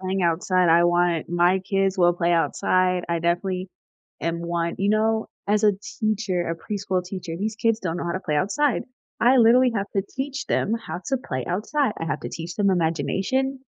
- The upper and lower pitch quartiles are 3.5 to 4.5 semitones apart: Yes, average, 3.9 semitones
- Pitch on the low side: No, medium, 185 Hz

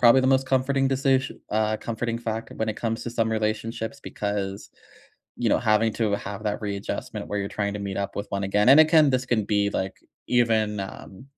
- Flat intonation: No, average, 3.4 semitones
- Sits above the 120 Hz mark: No, low, 110 Hz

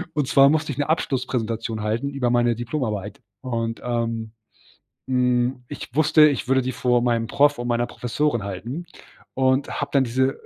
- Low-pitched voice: Yes, low, 125 Hz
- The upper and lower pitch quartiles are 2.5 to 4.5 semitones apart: Yes, average, 2.9 semitones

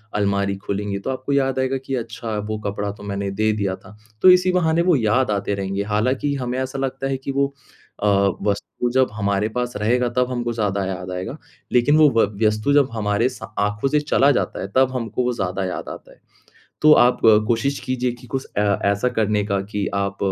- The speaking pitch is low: Yes, low, 115 Hz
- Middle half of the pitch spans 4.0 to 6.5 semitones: Yes, average, 4.5 semitones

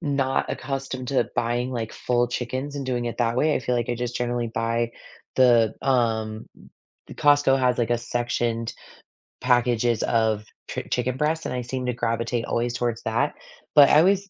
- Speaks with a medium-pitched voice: No, low, 120 Hz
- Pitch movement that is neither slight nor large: No, narrow, 2.0 semitones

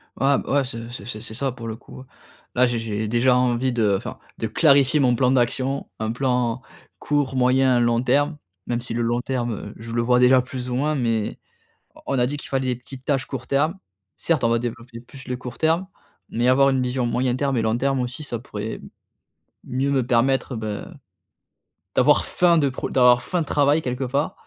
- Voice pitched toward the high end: No, low, 125 Hz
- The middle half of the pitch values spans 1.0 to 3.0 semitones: Yes, narrow, 2.4 semitones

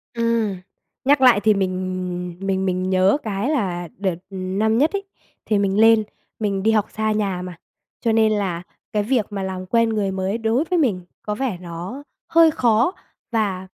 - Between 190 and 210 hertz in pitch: Yes, high, 205 Hz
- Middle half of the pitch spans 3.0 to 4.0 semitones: Yes, average, 3.3 semitones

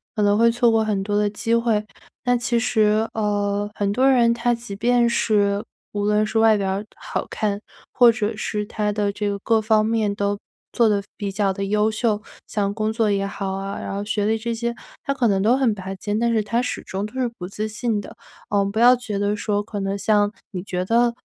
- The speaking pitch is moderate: No, high, 210 Hz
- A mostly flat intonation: Yes, narrow, 2.2 semitones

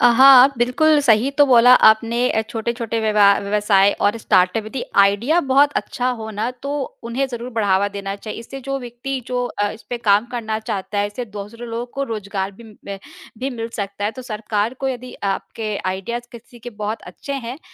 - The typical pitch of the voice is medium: No, high, 230 Hz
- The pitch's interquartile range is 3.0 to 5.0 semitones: Yes, average, 3.3 semitones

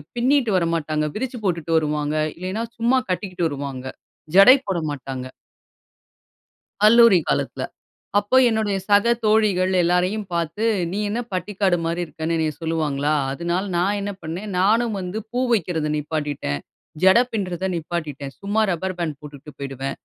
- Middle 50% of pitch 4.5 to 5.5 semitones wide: Yes, average, 5.1 semitones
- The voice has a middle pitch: Yes, medium, 180 Hz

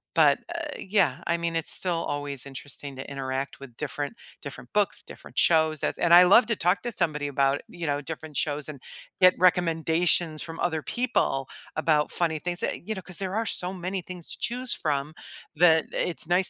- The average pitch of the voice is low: No, medium, 165 Hz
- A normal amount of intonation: Yes, average, 4.0 semitones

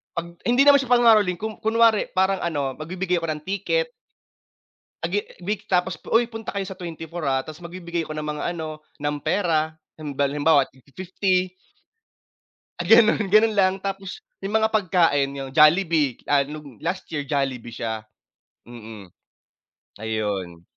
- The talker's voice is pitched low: No, medium, 170 Hz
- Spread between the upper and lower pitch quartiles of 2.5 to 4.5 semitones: No, wide, 5.4 semitones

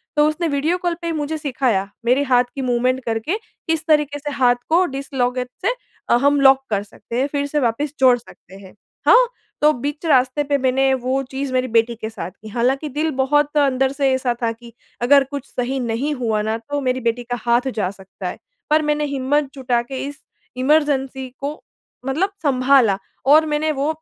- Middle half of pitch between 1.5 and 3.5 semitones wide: Yes, average, 3.2 semitones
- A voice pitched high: Yes, very high, 270 Hz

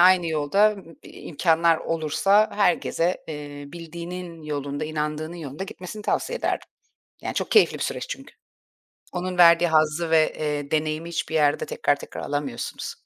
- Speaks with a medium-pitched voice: Yes, medium, 160 Hz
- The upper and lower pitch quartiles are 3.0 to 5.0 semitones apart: No, narrow, 2.5 semitones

